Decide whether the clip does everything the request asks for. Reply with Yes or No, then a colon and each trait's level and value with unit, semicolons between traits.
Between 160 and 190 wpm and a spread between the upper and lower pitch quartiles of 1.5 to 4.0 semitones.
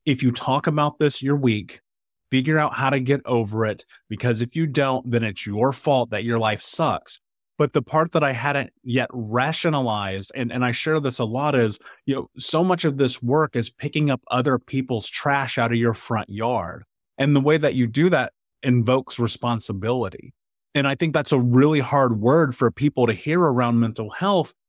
No: fast, 205 wpm; average, 3.5 semitones